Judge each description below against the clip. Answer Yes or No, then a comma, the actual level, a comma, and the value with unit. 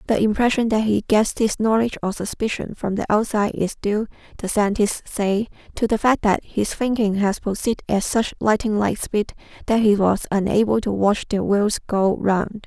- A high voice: Yes, high, 210 Hz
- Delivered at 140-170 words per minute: No, average, 190 wpm